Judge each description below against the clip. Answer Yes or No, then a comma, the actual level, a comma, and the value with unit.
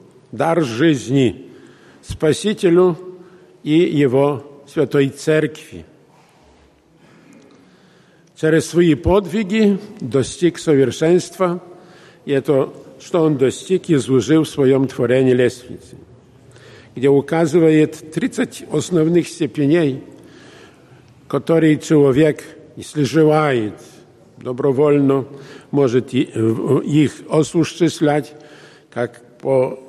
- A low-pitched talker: No, medium, 150 Hz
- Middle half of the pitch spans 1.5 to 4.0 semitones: Yes, average, 3.7 semitones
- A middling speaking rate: No, slow, 75 wpm